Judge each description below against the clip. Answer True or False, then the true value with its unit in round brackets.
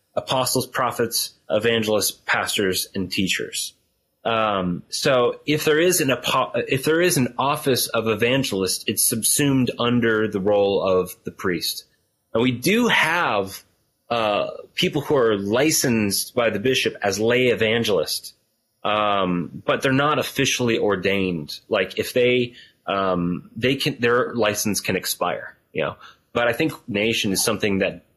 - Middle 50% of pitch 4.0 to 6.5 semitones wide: True (4.7 semitones)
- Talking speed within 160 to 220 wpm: False (145 wpm)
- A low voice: True (115 Hz)